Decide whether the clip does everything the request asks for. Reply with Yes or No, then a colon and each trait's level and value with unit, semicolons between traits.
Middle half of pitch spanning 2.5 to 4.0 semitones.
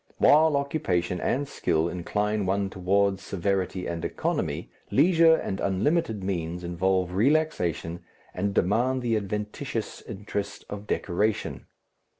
No: average, 4.5 semitones